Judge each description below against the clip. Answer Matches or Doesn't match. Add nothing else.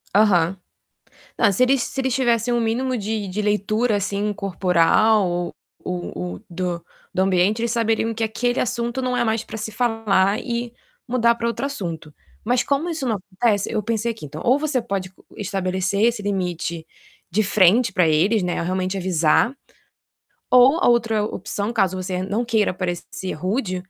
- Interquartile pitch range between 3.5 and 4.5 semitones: Matches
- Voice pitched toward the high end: Matches